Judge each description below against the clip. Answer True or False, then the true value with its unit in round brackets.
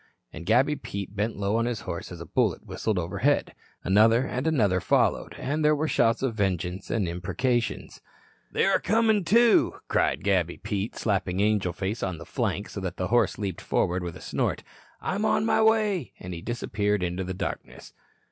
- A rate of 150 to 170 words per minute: False (185 wpm)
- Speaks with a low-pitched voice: True (105 Hz)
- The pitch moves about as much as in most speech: False (5.9 semitones)